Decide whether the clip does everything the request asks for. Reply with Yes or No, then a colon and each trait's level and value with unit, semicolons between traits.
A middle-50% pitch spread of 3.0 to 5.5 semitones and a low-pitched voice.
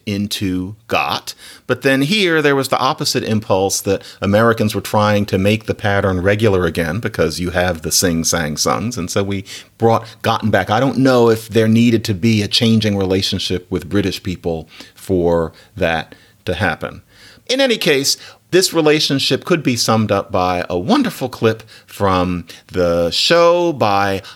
Yes: average, 4.2 semitones; low, 105 Hz